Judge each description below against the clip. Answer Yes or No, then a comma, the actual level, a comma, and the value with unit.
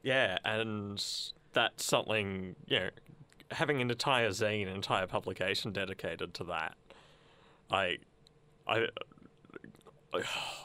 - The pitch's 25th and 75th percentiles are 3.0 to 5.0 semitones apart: Yes, average, 3.9 semitones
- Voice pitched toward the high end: No, low, 105 Hz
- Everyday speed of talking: No, slow, 115 wpm